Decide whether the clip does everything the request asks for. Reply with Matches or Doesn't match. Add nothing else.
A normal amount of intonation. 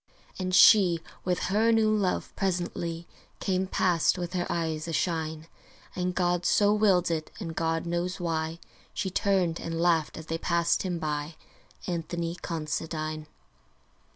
Doesn't match